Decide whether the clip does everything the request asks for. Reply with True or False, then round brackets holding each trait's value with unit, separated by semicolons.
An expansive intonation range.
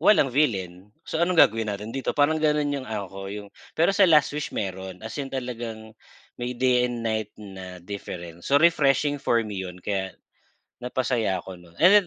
True (6.4 semitones)